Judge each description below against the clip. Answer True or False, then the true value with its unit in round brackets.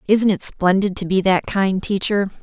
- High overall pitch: True (195 Hz)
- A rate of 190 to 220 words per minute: True (200 wpm)